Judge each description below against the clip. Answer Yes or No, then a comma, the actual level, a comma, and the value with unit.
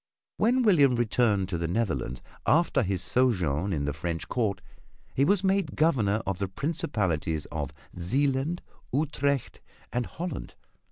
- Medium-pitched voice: No, low, 115 Hz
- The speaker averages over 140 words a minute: No, slow, 135 wpm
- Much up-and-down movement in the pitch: Yes, wide, 8.1 semitones